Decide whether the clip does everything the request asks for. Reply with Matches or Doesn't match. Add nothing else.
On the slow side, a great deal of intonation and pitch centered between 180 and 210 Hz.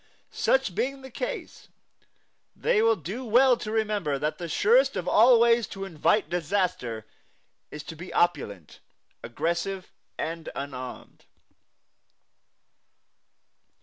Matches